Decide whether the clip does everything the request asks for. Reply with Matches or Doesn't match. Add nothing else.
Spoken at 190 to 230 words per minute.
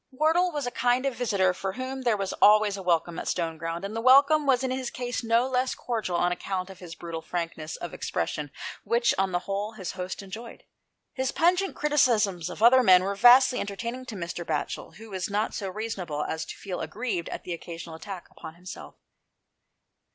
Matches